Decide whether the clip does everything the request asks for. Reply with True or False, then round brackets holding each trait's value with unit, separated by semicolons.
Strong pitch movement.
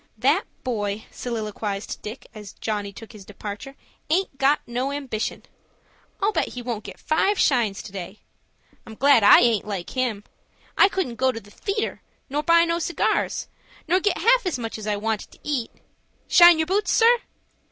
True (7.6 semitones)